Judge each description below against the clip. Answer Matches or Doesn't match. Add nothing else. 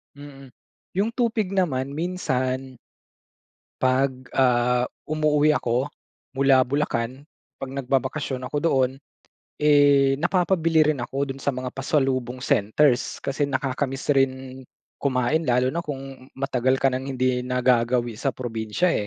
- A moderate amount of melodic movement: Doesn't match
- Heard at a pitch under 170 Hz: Matches